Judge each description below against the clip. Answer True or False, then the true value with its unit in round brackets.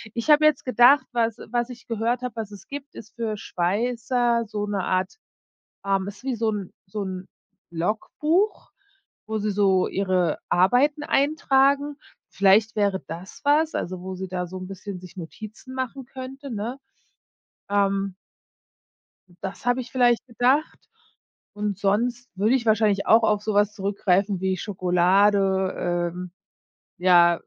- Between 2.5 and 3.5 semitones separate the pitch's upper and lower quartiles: False (4.4 semitones)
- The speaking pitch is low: False (210 Hz)